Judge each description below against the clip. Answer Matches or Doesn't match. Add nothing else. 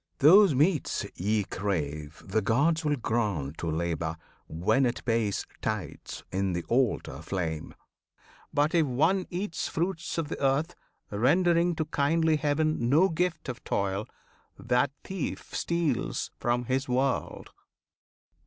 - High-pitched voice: Doesn't match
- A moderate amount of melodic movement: Doesn't match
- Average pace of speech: Doesn't match